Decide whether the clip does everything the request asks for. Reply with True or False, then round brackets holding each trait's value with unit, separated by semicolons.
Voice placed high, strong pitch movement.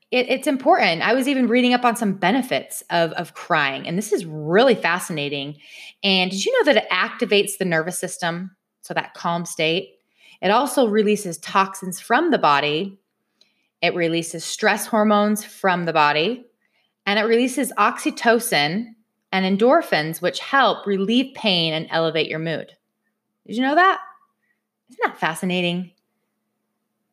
True (200 Hz; 5.7 semitones)